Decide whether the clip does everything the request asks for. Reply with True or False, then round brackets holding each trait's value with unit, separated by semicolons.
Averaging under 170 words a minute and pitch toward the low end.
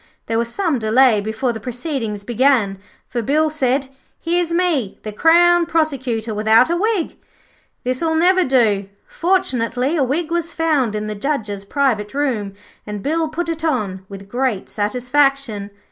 False (150 wpm; 260 Hz)